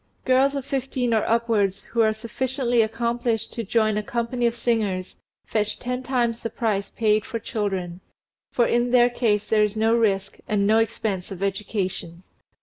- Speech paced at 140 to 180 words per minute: Yes, average, 170 wpm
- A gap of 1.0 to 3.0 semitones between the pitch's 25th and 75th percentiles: Yes, narrow, 2.5 semitones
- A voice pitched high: Yes, high, 225 Hz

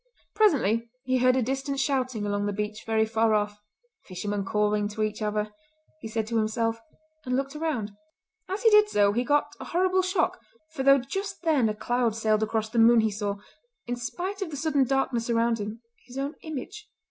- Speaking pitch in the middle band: No, high, 235 Hz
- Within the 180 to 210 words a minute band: Yes, average, 200 wpm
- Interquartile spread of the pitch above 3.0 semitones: Yes, average, 4.5 semitones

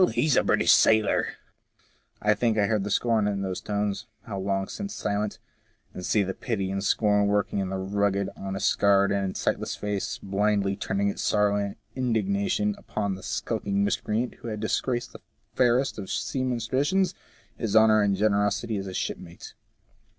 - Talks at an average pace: Yes, average, 180 wpm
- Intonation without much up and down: Yes, narrow, 1.9 semitones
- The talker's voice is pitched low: Yes, low, 105 Hz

